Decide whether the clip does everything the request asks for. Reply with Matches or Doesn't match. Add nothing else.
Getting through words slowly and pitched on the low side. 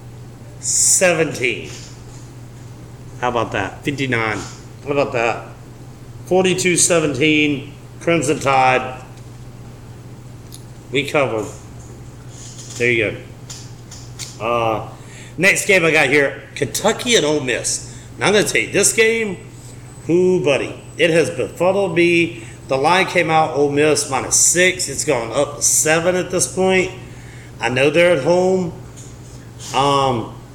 Matches